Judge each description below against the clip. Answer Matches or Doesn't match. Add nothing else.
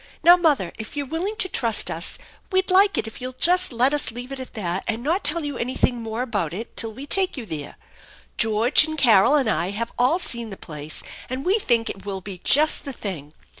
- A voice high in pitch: Matches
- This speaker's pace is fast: Matches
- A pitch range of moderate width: Doesn't match